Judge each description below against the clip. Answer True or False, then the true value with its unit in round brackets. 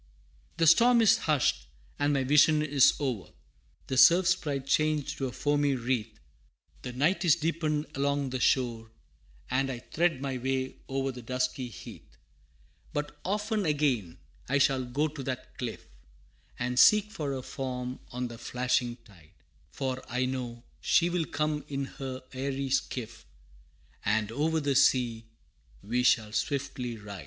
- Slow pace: False (155 wpm)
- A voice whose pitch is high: False (135 Hz)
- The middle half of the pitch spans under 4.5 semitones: True (3.1 semitones)